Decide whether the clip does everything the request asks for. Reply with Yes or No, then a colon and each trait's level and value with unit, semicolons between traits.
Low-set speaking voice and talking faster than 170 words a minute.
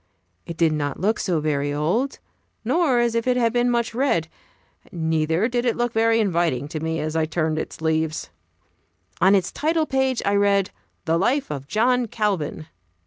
No: high, 195 Hz; average, 180 wpm